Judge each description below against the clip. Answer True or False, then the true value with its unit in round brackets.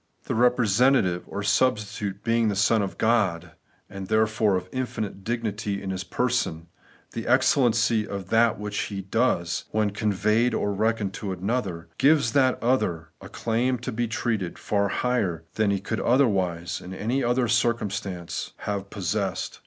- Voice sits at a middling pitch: False (105 Hz)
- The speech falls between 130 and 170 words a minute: True (155 wpm)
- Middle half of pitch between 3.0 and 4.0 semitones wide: True (3.4 semitones)